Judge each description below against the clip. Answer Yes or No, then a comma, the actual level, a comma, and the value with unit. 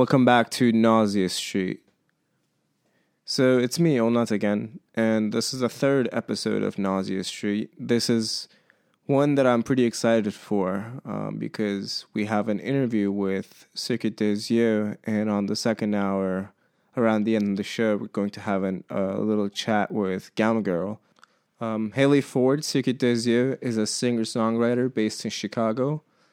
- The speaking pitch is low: Yes, low, 110 Hz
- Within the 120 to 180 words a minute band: Yes, average, 155 wpm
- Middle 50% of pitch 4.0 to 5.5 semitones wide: No, average, 2.9 semitones